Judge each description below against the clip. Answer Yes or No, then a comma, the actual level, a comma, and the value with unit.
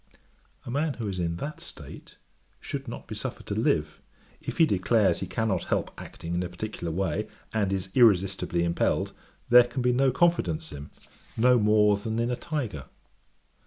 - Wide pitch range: Yes, wide, 5.7 semitones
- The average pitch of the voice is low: Yes, low, 105 Hz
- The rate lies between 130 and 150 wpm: No, average, 180 wpm